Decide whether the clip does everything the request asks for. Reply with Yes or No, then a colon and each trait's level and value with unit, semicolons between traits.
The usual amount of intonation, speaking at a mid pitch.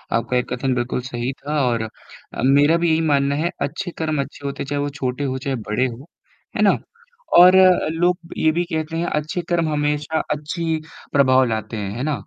Yes: average, 3.7 semitones; medium, 145 Hz